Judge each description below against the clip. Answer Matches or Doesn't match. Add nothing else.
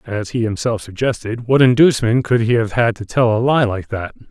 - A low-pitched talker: Matches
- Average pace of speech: Doesn't match